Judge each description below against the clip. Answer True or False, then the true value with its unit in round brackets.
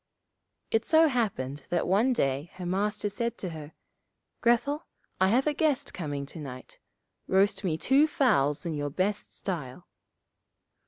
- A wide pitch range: True (8.1 semitones)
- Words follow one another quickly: False (150 wpm)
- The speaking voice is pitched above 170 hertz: True (190 Hz)